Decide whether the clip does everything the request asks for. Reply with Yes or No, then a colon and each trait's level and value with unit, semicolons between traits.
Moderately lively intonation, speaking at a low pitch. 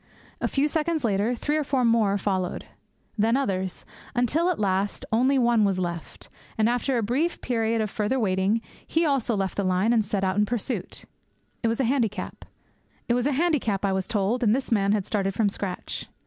No: average, 4.3 semitones; high, 225 Hz